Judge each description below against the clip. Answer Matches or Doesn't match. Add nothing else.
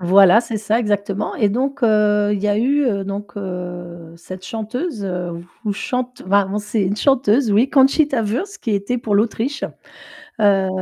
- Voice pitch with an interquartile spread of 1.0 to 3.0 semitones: Doesn't match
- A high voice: Matches